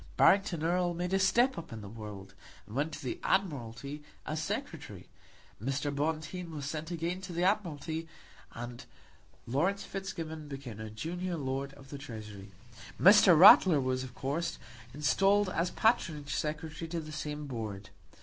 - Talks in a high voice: No, medium, 155 Hz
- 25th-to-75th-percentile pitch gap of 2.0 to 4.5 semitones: No, average, 4.9 semitones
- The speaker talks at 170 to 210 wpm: No, average, 155 wpm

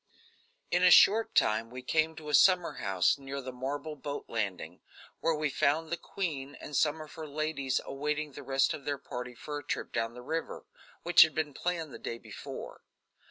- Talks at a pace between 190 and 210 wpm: Yes, average, 200 wpm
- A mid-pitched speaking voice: Yes, medium, 145 Hz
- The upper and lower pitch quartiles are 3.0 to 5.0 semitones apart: Yes, average, 3.3 semitones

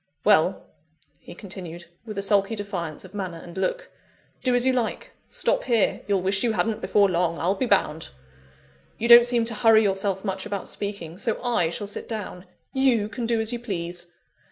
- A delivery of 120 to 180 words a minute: No, average, 190 wpm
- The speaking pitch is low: No, high, 205 Hz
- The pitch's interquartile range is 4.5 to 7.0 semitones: No, average, 3.8 semitones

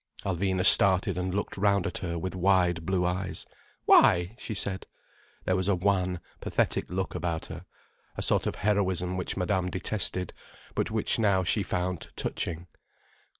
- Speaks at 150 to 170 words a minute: Yes, average, 155 wpm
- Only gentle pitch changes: Yes, narrow, 1.5 semitones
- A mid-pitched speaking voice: No, very low, 95 Hz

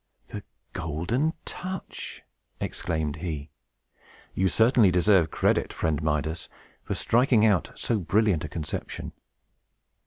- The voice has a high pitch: No, very low, 90 Hz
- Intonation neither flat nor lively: No, wide, 6.0 semitones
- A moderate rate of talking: No, slow, 105 wpm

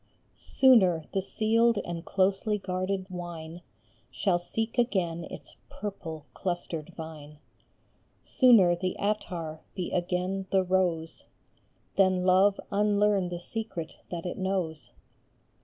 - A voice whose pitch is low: No, medium, 185 Hz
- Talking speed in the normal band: No, slow, 110 wpm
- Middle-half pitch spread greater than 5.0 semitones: No, average, 2.7 semitones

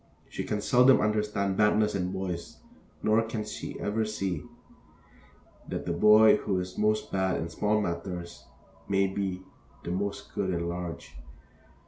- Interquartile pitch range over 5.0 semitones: No, average, 2.8 semitones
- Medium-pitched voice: No, low, 100 Hz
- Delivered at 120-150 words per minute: Yes, average, 140 wpm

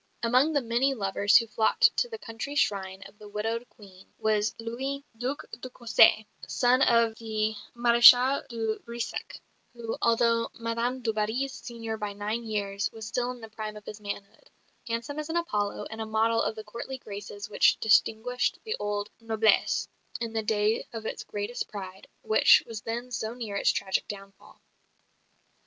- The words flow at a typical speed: Yes, average, 170 wpm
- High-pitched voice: Yes, high, 225 Hz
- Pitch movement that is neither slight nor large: No, narrow, 2.3 semitones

